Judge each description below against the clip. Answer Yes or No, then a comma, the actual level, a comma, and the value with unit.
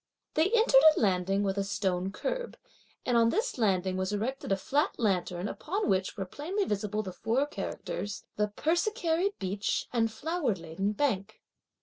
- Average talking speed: Yes, average, 160 wpm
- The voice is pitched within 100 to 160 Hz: No, high, 215 Hz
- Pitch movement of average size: No, wide, 8.0 semitones